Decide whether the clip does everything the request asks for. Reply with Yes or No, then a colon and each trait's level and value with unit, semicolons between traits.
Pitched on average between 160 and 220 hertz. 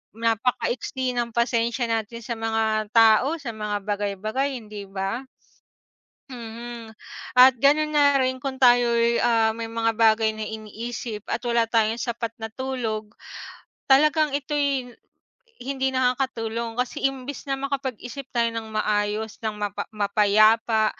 No: high, 230 Hz